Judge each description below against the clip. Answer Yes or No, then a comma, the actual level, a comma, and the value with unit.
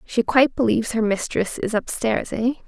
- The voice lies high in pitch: Yes, high, 225 Hz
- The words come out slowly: No, average, 200 wpm